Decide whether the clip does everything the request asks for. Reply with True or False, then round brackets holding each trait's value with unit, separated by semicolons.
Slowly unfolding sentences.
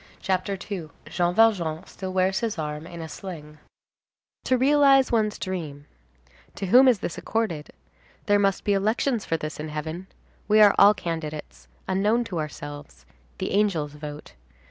False (150 wpm)